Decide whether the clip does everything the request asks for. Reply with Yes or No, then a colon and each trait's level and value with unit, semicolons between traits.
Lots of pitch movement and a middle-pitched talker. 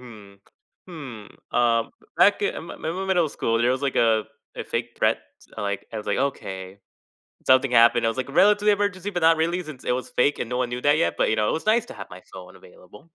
No: wide, 6.8 semitones; low, 125 Hz